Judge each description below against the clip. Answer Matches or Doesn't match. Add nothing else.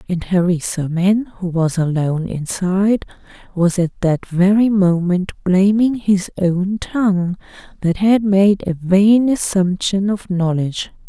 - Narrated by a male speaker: Doesn't match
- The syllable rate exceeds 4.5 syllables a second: Doesn't match